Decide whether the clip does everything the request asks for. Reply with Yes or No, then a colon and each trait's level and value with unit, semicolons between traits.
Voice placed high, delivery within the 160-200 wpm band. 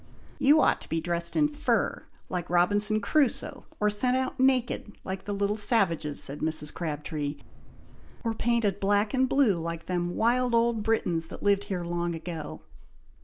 Yes: high, 200 Hz; average, 165 wpm